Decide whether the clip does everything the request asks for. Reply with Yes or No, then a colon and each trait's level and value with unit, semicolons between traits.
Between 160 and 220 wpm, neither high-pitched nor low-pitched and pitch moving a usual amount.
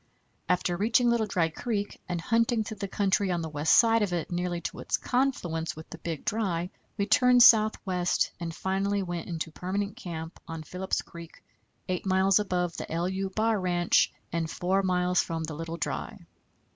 Yes: average, 180 wpm; medium, 180 Hz; average, 3.3 semitones